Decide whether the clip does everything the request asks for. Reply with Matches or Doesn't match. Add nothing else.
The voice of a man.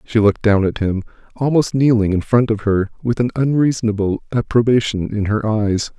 Matches